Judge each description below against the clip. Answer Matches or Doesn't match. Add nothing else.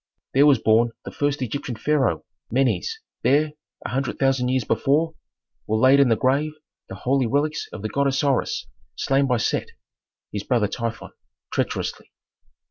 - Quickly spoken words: Doesn't match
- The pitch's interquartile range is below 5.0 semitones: Matches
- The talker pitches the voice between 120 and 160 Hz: Matches